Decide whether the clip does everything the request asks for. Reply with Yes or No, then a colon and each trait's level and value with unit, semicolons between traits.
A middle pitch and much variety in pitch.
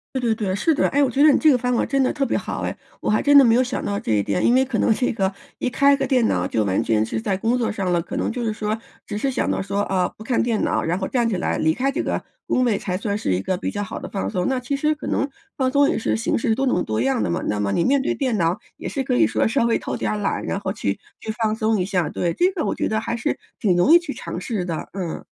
No: high, 220 Hz; wide, 6.0 semitones